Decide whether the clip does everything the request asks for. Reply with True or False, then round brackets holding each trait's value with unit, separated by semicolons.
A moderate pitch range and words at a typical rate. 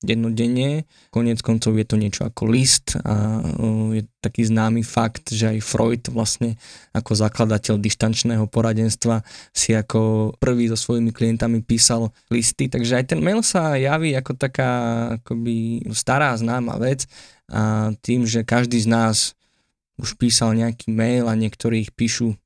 False (1.4 semitones; 145 wpm)